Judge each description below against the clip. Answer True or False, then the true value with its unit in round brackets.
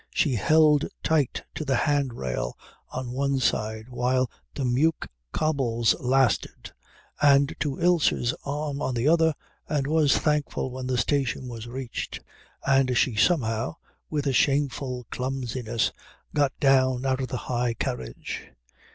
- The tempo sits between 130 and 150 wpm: True (140 wpm)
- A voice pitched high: False (130 Hz)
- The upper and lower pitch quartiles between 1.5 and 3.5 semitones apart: True (2.8 semitones)